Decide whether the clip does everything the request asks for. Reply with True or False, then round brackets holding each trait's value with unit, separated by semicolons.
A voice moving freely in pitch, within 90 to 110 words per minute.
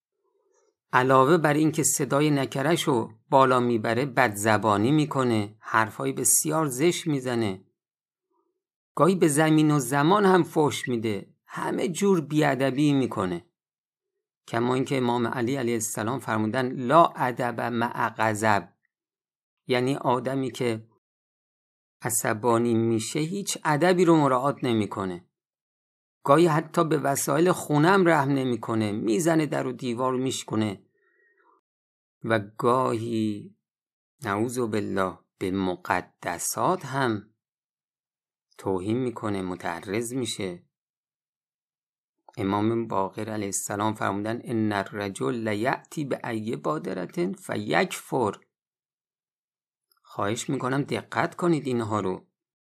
True (5.7 semitones; 105 wpm)